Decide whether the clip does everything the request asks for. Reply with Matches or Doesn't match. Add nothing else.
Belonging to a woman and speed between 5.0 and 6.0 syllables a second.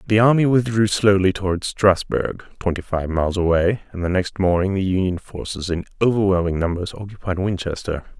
Doesn't match